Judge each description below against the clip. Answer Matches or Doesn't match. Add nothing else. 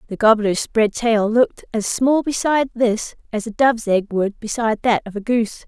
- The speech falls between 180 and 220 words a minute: Matches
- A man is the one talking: Doesn't match